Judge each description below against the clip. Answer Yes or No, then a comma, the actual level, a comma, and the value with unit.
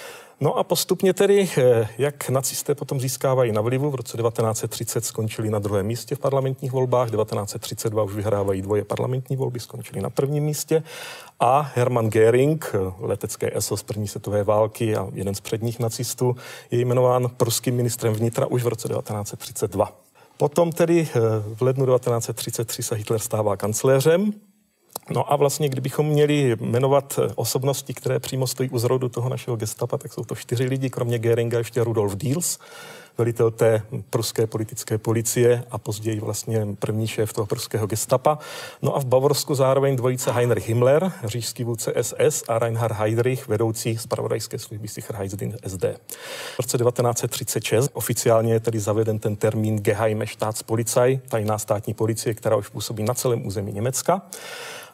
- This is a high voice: No, low, 120 Hz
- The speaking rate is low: No, average, 155 wpm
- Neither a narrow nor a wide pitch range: Yes, average, 3.1 semitones